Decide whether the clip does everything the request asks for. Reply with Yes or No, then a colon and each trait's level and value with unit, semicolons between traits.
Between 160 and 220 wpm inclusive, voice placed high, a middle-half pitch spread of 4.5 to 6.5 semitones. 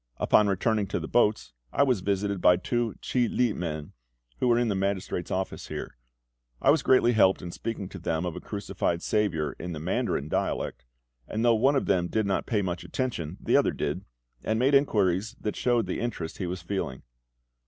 No: average, 200 wpm; low, 100 Hz; average, 4.9 semitones